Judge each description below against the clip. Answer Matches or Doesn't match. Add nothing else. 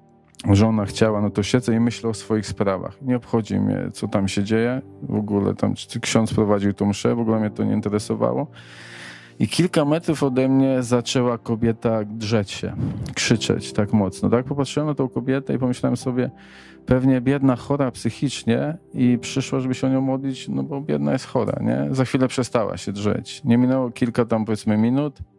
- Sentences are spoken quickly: Matches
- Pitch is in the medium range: Doesn't match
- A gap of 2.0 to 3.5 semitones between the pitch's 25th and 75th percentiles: Doesn't match